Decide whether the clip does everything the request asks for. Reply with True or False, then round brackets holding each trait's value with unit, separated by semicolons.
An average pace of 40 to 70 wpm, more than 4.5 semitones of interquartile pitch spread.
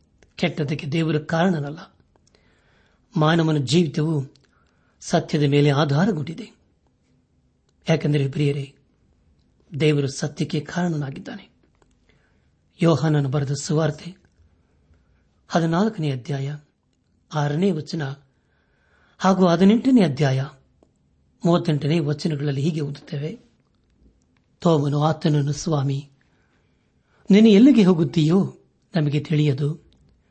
False (65 wpm; 3.2 semitones)